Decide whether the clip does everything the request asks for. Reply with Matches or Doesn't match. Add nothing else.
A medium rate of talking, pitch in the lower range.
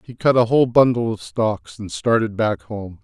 Doesn't match